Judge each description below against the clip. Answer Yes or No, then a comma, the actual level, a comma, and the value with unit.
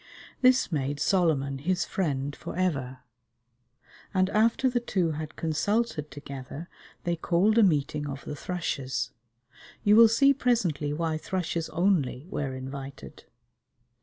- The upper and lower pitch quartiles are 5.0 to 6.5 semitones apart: Yes, wide, 5.5 semitones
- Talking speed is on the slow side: Yes, slow, 130 wpm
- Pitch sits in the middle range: Yes, medium, 160 Hz